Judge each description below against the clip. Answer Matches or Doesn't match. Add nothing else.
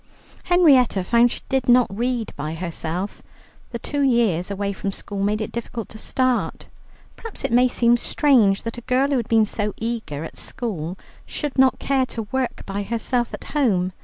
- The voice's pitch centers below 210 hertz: Doesn't match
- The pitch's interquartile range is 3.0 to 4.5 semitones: Matches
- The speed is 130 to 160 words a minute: Doesn't match